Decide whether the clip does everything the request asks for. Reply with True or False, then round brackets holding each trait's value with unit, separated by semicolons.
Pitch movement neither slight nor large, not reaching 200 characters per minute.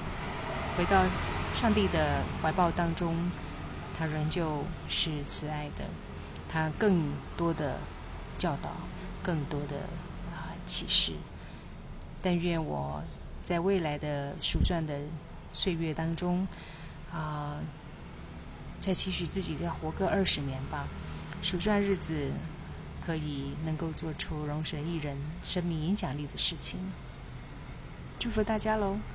True (3.7 semitones; 175 characters per minute)